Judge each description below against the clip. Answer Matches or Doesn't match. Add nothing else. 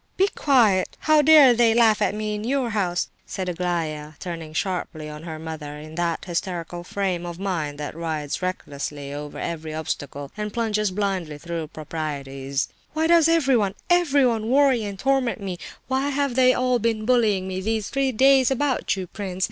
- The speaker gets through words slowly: Doesn't match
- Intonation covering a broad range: Matches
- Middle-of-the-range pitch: Doesn't match